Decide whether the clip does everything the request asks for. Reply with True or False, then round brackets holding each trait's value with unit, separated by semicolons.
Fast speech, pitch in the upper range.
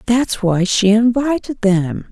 False (140 wpm; 220 Hz)